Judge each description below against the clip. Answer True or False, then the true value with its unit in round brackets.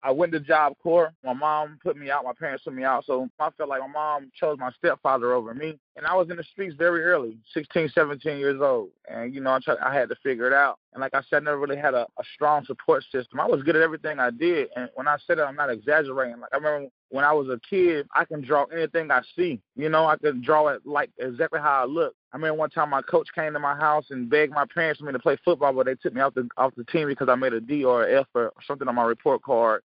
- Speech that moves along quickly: True (290 wpm)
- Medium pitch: True (150 Hz)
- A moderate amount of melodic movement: True (3.5 semitones)